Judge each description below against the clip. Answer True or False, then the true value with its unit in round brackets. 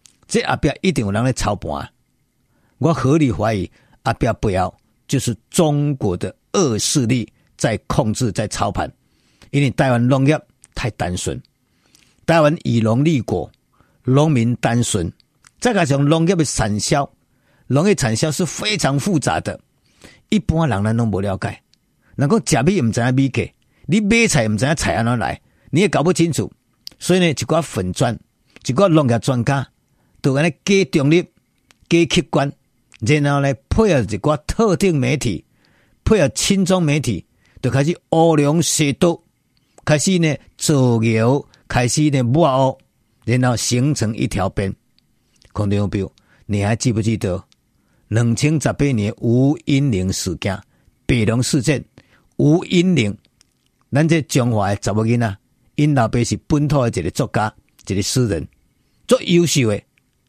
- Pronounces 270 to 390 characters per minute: False (220 characters per minute)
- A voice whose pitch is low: True (130 Hz)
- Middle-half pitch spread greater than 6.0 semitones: False (5.6 semitones)